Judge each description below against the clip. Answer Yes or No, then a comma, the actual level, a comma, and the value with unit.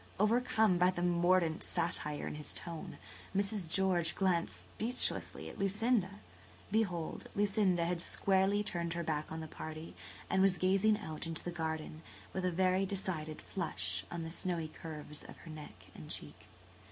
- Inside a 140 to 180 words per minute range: Yes, average, 160 wpm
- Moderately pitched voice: Yes, medium, 175 Hz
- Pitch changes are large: No, average, 3.3 semitones